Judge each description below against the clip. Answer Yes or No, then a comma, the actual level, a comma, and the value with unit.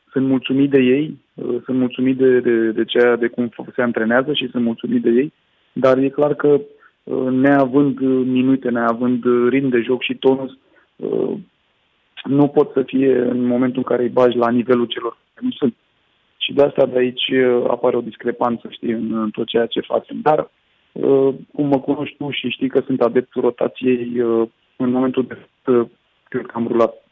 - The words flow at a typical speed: No, fast, 195 wpm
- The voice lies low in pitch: Yes, low, 125 Hz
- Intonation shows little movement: Yes, narrow, 1.8 semitones